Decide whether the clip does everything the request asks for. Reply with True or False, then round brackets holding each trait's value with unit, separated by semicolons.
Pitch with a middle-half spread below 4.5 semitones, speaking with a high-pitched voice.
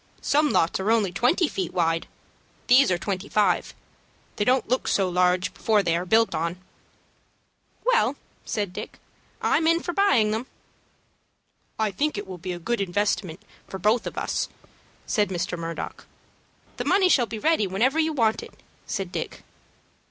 False (5.6 semitones; 210 Hz)